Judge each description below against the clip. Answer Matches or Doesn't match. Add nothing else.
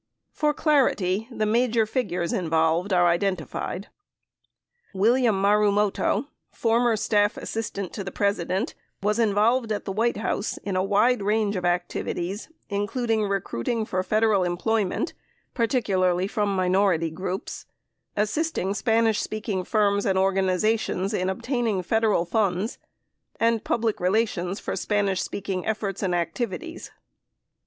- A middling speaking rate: Doesn't match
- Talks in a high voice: Matches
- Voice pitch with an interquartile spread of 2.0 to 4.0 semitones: Matches